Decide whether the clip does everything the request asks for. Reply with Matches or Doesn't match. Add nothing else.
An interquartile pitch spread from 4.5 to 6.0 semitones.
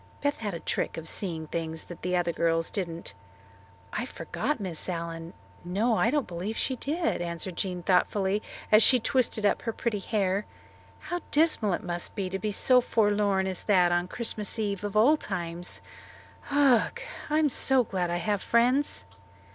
Matches